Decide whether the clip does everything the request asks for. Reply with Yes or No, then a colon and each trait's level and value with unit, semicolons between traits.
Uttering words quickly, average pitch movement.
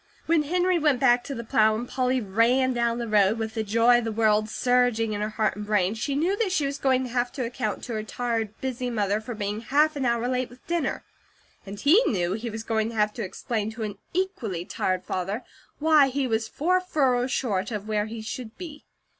Yes: fast, 230 wpm; average, 3.6 semitones